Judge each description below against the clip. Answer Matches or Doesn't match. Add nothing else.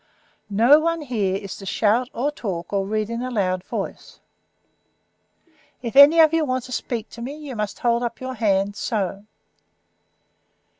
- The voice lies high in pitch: Matches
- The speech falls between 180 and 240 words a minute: Doesn't match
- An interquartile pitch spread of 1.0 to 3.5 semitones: Doesn't match